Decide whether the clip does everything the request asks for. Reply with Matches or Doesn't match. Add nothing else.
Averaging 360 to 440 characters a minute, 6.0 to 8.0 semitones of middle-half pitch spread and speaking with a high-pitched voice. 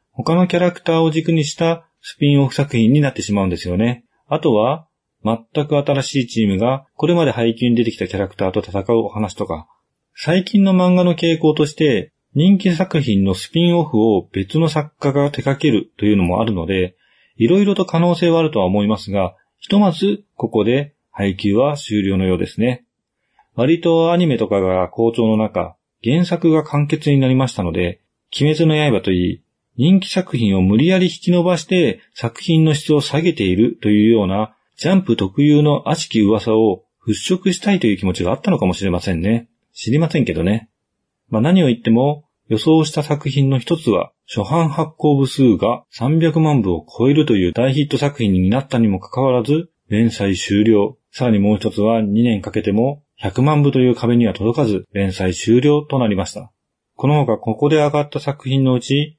Doesn't match